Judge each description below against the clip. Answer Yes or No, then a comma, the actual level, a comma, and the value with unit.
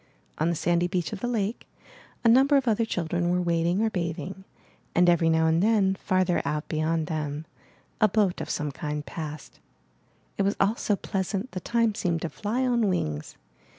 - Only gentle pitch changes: No, average, 4.6 semitones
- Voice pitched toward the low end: No, medium, 180 Hz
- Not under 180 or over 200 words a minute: Yes, average, 185 wpm